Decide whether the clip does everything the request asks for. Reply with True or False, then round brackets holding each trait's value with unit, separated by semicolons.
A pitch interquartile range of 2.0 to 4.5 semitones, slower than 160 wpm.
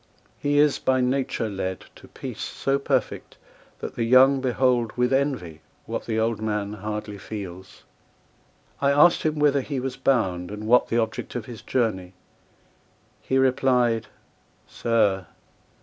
True (4.0 semitones; 145 wpm)